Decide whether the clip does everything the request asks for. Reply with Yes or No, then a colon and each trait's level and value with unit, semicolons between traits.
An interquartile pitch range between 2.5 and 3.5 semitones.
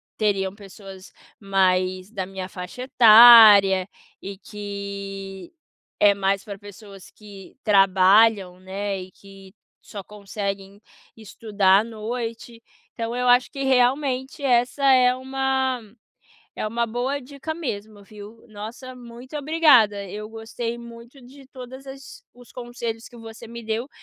No: average, 3.9 semitones